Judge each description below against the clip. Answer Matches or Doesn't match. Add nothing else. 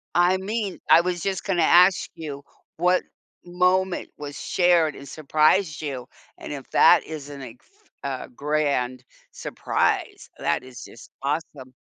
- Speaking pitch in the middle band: Matches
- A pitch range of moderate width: Matches